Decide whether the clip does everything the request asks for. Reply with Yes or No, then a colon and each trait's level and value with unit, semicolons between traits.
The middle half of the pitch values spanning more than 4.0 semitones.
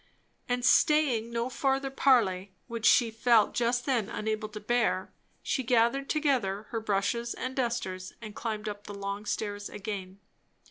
No: average, 3.2 semitones